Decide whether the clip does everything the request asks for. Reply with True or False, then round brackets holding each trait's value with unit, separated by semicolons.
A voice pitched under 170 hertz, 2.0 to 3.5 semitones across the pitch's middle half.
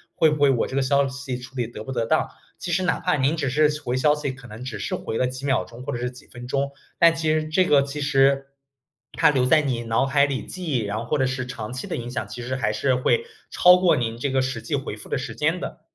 True (135 Hz; 3.0 semitones)